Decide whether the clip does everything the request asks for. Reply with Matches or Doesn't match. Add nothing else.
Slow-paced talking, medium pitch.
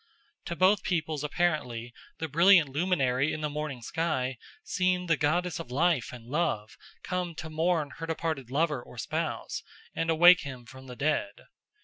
Doesn't match